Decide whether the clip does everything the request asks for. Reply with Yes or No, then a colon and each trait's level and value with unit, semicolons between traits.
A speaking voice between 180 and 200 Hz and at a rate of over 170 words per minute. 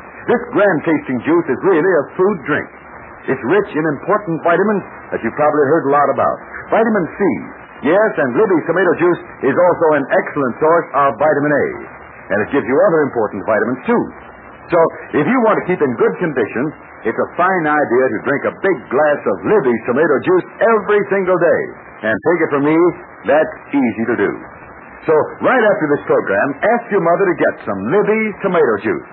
Yes: medium, 185 Hz; average, 190 wpm